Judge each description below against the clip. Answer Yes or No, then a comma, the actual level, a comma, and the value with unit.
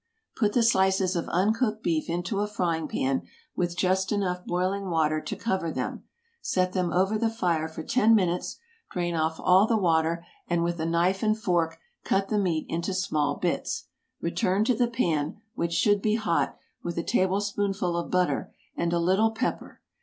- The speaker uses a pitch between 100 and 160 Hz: No, medium, 185 Hz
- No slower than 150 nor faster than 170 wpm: No, average, 180 wpm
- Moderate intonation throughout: Yes, average, 3.3 semitones